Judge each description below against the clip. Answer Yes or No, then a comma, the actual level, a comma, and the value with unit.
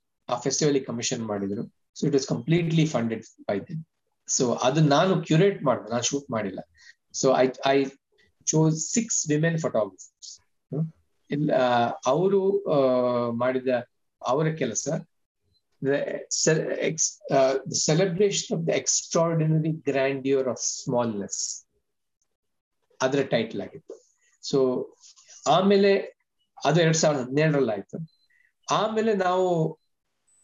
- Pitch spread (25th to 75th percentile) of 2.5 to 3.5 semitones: No, wide, 5.5 semitones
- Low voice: No, medium, 145 Hz